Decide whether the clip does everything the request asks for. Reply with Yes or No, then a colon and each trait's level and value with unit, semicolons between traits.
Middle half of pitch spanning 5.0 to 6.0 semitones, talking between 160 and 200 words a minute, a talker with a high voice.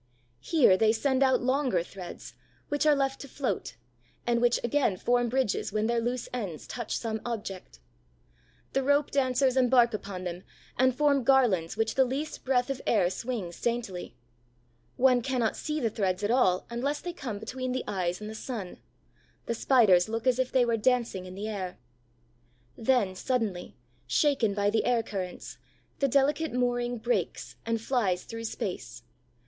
No: average, 4.2 semitones; average, 165 wpm; high, 235 Hz